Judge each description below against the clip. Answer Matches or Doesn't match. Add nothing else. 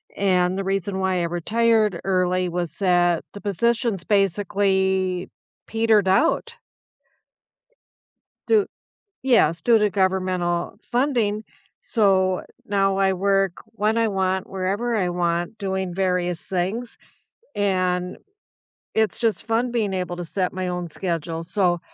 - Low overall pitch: Doesn't match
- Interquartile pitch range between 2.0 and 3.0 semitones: Matches